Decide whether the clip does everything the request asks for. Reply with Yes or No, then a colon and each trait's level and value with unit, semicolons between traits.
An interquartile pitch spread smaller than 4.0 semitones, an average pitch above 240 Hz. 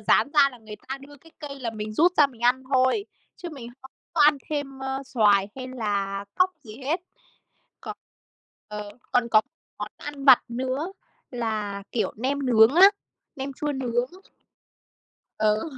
No: average, 4.3 semitones; very high, 260 Hz